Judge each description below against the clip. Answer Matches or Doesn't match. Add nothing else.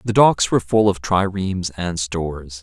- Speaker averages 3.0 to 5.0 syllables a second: Matches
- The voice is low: Matches